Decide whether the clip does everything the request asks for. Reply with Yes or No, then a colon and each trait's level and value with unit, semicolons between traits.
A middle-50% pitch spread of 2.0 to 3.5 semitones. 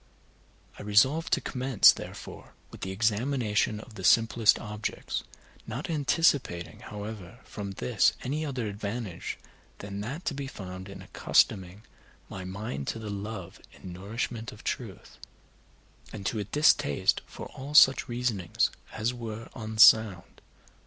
No: average, 3.9 semitones